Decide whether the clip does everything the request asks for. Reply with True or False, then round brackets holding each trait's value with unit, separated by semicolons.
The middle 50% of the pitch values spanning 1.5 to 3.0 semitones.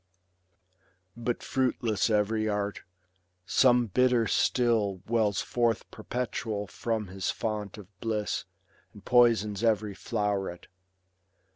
True (2.4 semitones)